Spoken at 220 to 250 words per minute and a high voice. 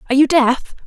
No: fast, 205 wpm; very high, 275 Hz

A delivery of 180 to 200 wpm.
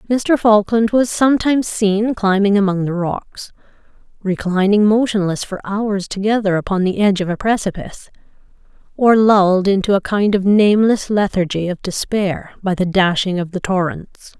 No: average, 150 wpm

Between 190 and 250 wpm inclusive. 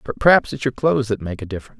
No: fast, 270 wpm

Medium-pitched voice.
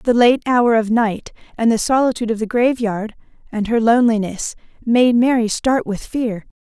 No: high, 230 Hz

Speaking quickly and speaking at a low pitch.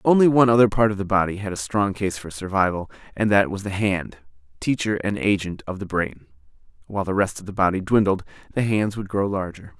Yes: fast, 220 wpm; low, 100 Hz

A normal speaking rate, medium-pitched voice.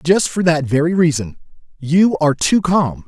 Yes: average, 175 wpm; medium, 160 Hz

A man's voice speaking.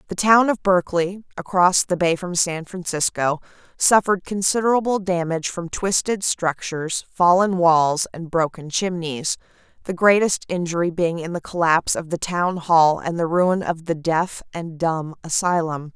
No: female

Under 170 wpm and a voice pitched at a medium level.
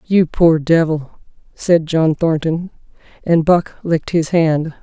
Yes: slow, 135 wpm; medium, 165 Hz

